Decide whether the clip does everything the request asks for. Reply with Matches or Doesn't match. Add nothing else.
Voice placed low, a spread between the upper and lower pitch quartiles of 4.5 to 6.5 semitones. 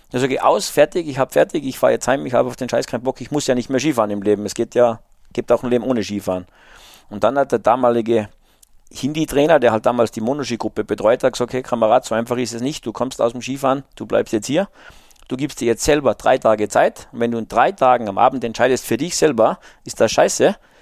Doesn't match